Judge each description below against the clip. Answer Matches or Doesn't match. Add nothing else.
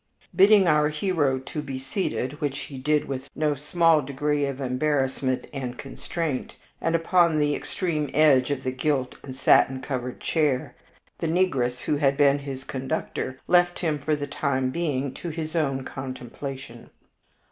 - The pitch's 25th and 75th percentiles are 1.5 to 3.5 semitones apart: Matches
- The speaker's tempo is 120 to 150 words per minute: Doesn't match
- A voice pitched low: Doesn't match